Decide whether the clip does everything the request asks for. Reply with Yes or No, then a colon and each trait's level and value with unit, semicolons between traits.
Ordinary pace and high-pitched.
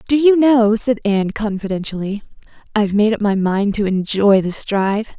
Yes: average, 175 wpm; high, 210 Hz